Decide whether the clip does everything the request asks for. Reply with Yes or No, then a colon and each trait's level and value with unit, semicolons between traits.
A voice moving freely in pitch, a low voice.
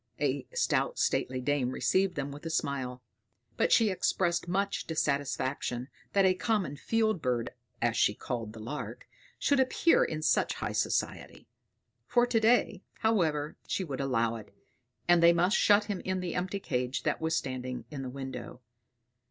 No: wide, 7.1 semitones; medium, 160 Hz